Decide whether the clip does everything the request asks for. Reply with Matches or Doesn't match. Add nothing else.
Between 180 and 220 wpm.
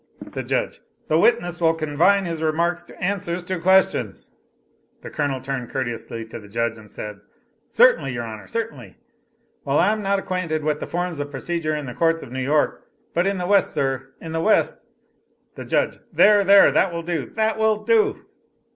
Matches